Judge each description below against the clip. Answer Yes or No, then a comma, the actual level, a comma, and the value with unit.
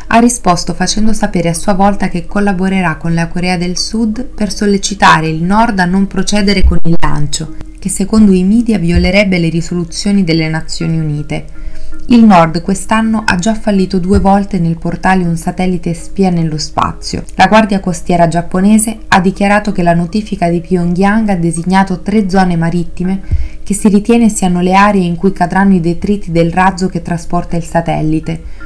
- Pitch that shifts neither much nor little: Yes, average, 3.0 semitones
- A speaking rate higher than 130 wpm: Yes, fast, 170 wpm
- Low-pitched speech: No, medium, 185 Hz